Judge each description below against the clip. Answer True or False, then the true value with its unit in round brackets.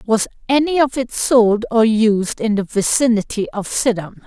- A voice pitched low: False (225 Hz)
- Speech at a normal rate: True (170 wpm)